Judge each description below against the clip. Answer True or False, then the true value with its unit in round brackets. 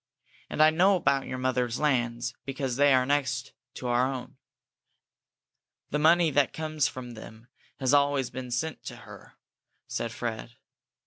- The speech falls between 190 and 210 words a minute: False (150 wpm)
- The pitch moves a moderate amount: True (3.0 semitones)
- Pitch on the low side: True (130 Hz)